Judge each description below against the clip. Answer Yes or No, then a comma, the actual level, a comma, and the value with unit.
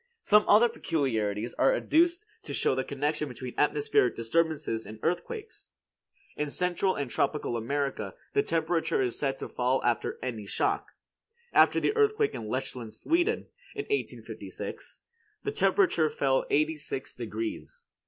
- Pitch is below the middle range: No, medium, 145 Hz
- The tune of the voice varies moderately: No, wide, 8.8 semitones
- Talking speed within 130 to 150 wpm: Yes, average, 140 wpm